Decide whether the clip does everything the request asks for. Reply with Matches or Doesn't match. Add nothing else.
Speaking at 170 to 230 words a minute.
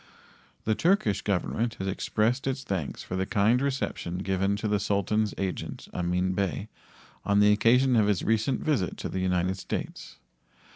Doesn't match